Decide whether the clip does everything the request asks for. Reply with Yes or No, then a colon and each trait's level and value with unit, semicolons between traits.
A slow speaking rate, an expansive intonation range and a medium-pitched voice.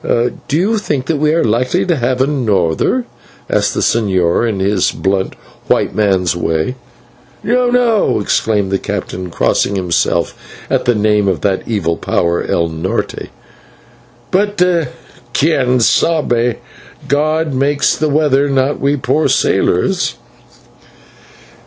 No: slow, 130 wpm; wide, 7.5 semitones; low, 120 Hz